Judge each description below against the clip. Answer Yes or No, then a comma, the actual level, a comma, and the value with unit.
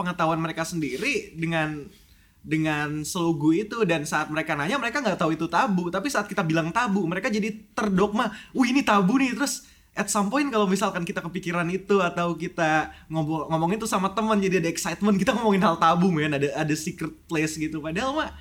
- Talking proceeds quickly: Yes, fast, 190 wpm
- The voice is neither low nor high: Yes, medium, 175 Hz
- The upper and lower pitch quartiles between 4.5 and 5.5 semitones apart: Yes, average, 4.8 semitones